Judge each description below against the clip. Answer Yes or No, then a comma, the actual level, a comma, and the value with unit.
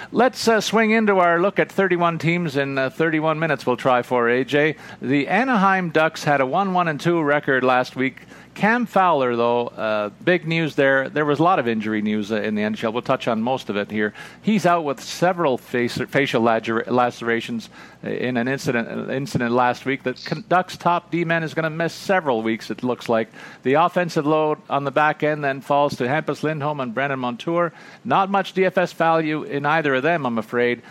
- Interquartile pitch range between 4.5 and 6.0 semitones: Yes, wide, 5.6 semitones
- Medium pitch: Yes, medium, 145 Hz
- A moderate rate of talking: No, fast, 210 wpm